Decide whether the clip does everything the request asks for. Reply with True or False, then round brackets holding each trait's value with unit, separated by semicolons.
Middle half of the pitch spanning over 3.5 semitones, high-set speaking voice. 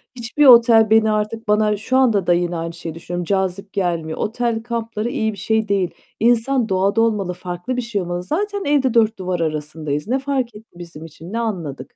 True (4.8 semitones; 210 Hz)